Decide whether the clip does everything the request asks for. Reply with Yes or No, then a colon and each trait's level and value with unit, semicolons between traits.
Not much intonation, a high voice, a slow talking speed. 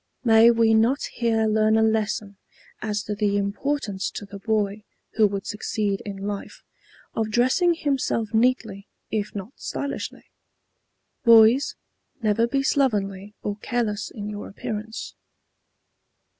Yes: narrow, 2.3 semitones; high, 220 Hz; slow, 130 wpm